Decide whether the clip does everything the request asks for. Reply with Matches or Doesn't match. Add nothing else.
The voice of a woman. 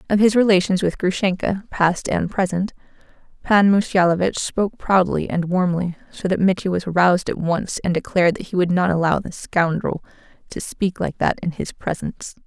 Matches